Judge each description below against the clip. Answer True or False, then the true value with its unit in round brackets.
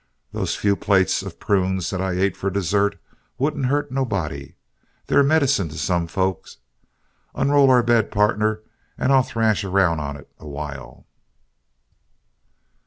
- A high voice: False (100 Hz)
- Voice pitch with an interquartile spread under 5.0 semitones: False (5.5 semitones)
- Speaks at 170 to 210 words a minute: False (135 wpm)